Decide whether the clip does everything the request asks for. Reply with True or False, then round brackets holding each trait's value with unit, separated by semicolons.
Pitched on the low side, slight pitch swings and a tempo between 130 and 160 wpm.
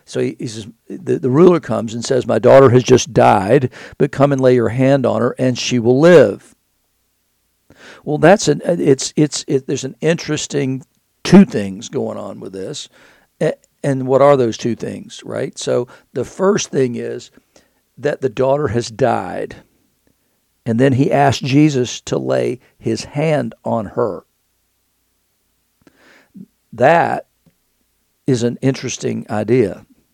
False (130 Hz; 3.5 semitones; 145 wpm)